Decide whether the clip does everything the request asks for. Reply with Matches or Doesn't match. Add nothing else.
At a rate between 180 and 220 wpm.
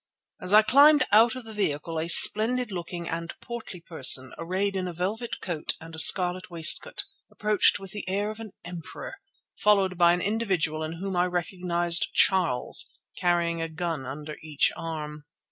Doesn't match